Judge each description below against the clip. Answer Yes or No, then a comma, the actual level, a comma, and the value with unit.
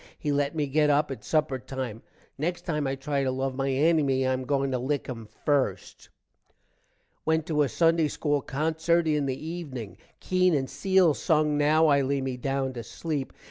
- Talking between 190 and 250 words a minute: Yes, average, 195 wpm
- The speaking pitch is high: No, medium, 145 Hz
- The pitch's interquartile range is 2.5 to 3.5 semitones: Yes, average, 2.8 semitones